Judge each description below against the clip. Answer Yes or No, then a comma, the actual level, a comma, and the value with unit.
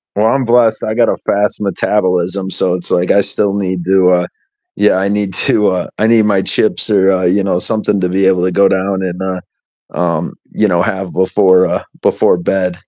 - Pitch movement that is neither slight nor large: No, narrow, 2.1 semitones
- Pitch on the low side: Yes, very low, 95 Hz